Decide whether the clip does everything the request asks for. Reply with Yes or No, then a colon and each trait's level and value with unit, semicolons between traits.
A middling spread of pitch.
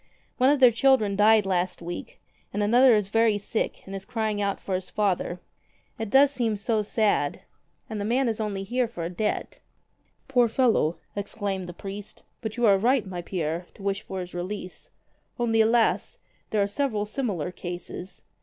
Yes: average, 3.3 semitones